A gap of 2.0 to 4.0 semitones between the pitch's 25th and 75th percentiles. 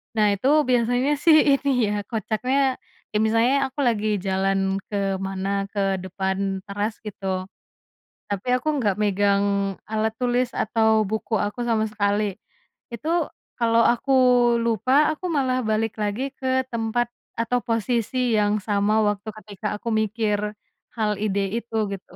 Yes: average, 3.3 semitones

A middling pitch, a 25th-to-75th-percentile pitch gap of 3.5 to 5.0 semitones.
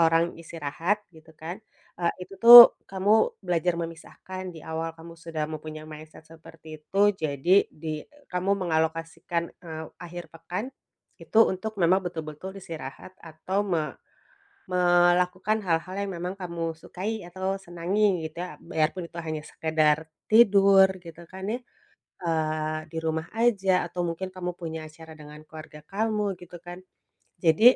No: medium, 170 Hz; average, 2.7 semitones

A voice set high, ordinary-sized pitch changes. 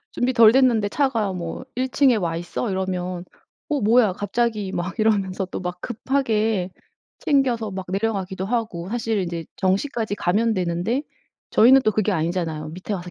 Yes: high, 205 Hz; average, 4.2 semitones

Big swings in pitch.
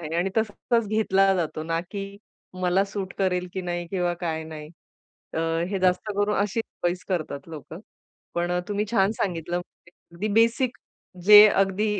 No: average, 2.9 semitones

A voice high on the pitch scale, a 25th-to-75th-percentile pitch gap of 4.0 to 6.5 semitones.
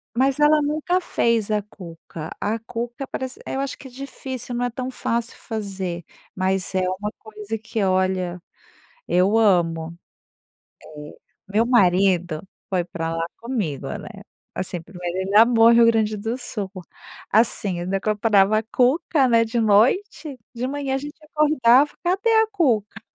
Yes: high, 220 Hz; wide, 5.4 semitones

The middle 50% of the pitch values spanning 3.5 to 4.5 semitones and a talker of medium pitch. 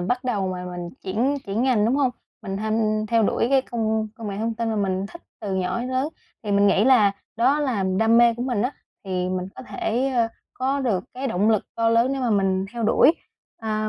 No: average, 4.0 semitones; high, 225 Hz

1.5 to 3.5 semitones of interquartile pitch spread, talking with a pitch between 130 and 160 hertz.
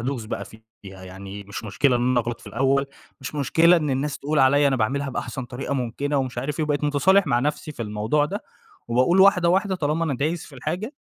No: average, 4.0 semitones; medium, 140 Hz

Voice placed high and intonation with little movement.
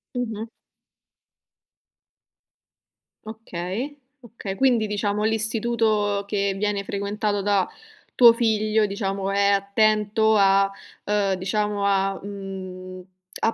Yes: high, 205 Hz; narrow, 1.8 semitones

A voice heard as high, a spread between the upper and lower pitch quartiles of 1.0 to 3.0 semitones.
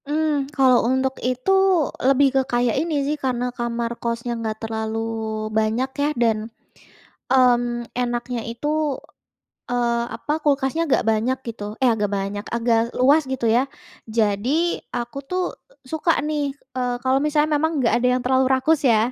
Yes: high, 245 Hz; narrow, 2.4 semitones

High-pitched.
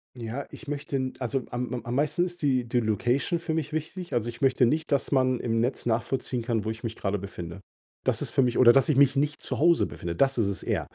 No: low, 125 Hz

